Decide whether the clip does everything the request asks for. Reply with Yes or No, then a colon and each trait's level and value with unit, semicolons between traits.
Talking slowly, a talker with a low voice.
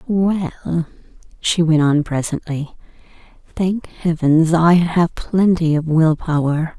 No: slow, 115 wpm; medium, 165 Hz